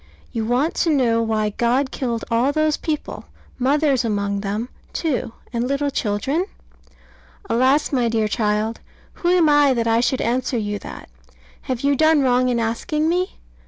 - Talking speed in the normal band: Yes, average, 160 wpm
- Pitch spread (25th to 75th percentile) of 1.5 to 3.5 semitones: No, average, 4.1 semitones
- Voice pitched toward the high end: Yes, very high, 250 Hz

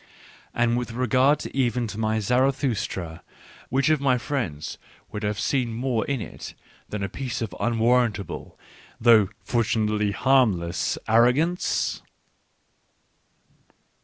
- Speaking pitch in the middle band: No, low, 120 Hz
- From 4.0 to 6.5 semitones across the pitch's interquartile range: No, average, 3.4 semitones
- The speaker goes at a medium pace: No, slow, 115 wpm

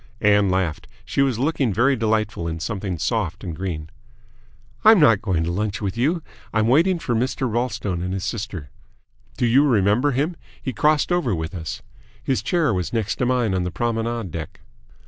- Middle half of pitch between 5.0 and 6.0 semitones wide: Yes, wide, 5.6 semitones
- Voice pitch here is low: Yes, low, 110 Hz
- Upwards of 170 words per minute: Yes, average, 185 wpm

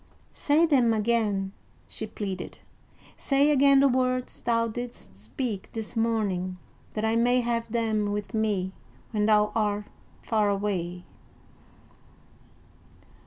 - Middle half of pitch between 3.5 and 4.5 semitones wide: No, average, 2.9 semitones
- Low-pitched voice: No, high, 220 Hz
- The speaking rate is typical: No, slow, 120 wpm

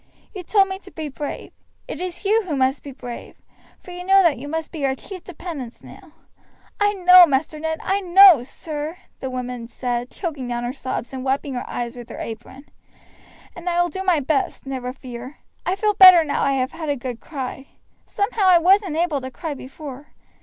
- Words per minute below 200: No, fast, 205 wpm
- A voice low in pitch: No, very high, 295 Hz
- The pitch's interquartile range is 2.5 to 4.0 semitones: No, wide, 5.6 semitones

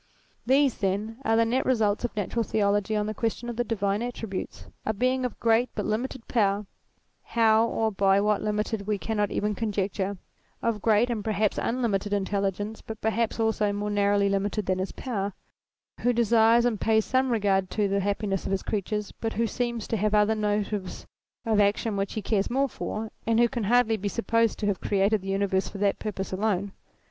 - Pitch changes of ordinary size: No, narrow, 2.2 semitones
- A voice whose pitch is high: Yes, high, 210 Hz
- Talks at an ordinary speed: Yes, average, 195 wpm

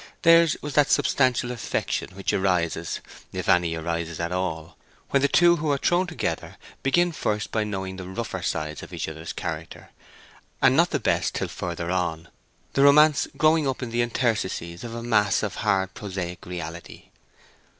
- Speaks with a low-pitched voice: Yes, low, 100 Hz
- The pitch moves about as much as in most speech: No, wide, 7.9 semitones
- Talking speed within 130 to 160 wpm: No, average, 170 wpm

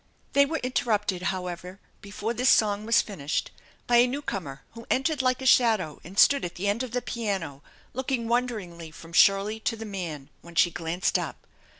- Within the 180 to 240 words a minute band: Yes, average, 185 wpm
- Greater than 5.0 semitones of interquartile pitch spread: Yes, wide, 5.6 semitones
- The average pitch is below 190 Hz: No, high, 205 Hz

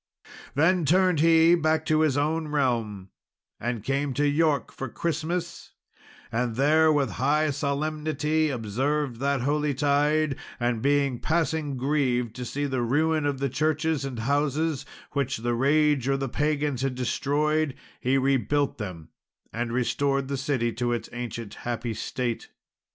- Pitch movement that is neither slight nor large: Yes, average, 3.6 semitones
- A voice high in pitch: No, medium, 140 Hz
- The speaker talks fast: No, average, 145 wpm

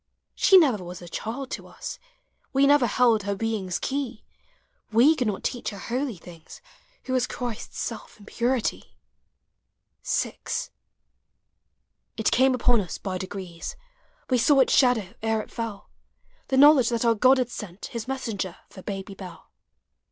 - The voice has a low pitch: No, high, 230 Hz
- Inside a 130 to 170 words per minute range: Yes, average, 160 wpm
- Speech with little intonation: No, average, 4.4 semitones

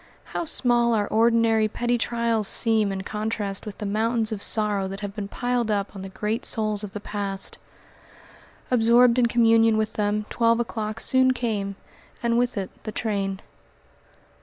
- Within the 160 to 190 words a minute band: Yes, average, 165 wpm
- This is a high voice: Yes, high, 220 Hz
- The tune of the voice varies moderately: No, narrow, 2.2 semitones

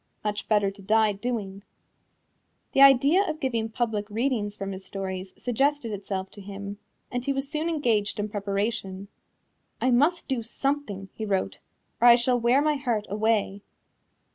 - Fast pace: No, average, 160 wpm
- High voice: Yes, high, 220 Hz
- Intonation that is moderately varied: Yes, average, 4.3 semitones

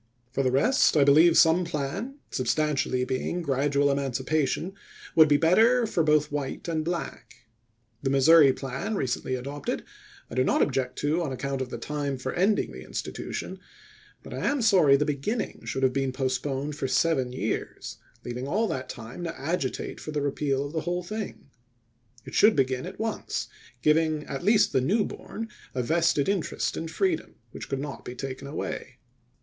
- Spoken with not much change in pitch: No, average, 4.1 semitones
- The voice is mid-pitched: Yes, medium, 145 Hz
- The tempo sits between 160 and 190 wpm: Yes, average, 175 wpm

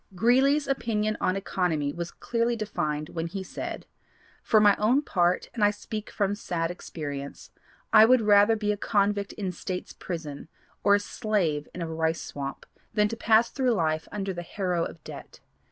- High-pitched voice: Yes, high, 200 Hz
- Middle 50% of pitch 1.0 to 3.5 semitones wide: No, average, 4.4 semitones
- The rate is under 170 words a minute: No, average, 175 wpm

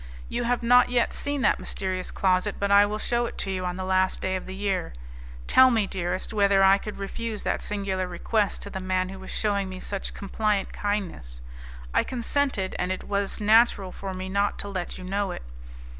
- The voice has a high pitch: Yes, high, 200 Hz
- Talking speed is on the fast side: Yes, fast, 210 wpm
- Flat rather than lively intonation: Yes, narrow, 2.1 semitones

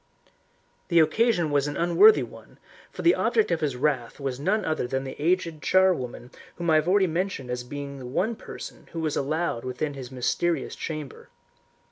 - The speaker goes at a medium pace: Yes, average, 180 wpm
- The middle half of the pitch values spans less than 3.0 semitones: No, average, 4.8 semitones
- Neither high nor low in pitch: Yes, medium, 155 Hz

